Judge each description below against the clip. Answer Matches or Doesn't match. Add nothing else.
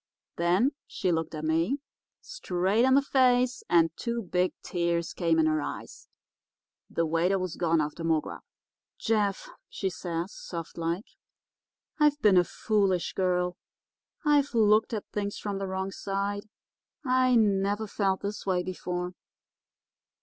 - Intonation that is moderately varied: Matches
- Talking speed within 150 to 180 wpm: Doesn't match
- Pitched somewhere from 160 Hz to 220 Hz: Matches